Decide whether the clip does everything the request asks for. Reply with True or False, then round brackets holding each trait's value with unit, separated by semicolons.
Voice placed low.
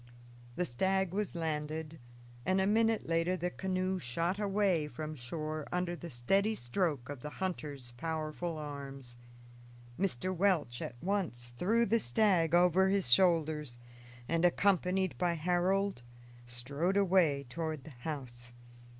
False (165 Hz)